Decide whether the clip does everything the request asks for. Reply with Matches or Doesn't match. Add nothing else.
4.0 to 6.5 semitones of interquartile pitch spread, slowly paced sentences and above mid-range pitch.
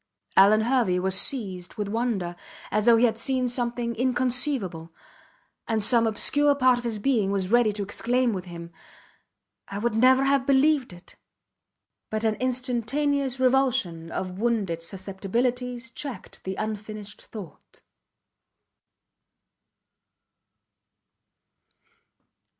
Matches